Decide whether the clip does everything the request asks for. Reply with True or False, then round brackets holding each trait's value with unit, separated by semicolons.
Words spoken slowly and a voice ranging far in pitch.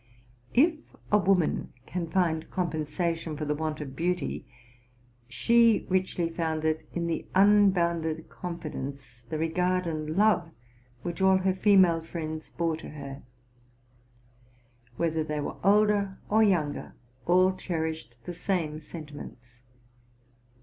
False (125 wpm; 3.2 semitones)